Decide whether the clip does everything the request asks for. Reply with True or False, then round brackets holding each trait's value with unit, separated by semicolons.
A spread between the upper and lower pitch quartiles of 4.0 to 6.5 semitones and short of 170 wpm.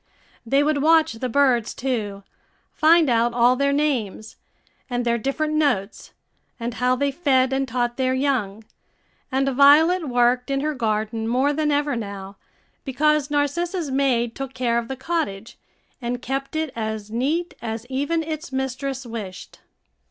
False (3.6 semitones; 150 wpm)